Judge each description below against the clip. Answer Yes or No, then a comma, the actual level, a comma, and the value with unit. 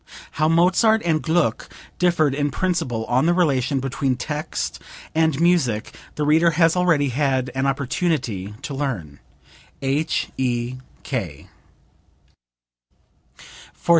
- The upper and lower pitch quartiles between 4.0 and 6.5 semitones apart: Yes, average, 4.4 semitones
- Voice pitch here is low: No, medium, 145 Hz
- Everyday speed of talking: No, slow, 105 wpm